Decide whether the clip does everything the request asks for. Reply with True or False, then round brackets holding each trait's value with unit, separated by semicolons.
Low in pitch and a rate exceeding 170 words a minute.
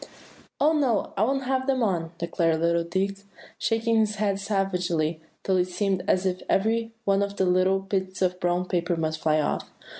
False (190 Hz; 185 wpm)